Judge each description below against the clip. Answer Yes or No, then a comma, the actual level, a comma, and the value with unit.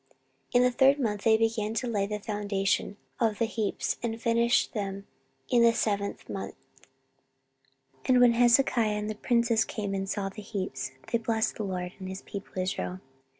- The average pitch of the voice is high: Yes, high, 215 Hz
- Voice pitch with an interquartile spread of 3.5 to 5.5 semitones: No, average, 2.8 semitones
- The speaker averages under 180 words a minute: No, average, 185 wpm